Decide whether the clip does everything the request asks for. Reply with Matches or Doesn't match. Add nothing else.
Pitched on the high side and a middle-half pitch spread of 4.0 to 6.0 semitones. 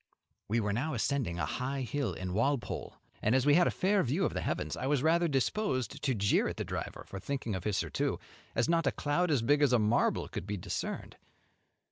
Doesn't match